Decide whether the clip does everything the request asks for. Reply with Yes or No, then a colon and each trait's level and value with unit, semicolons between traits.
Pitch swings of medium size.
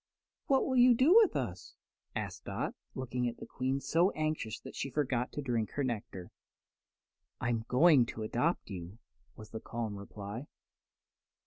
No: wide, 5.7 semitones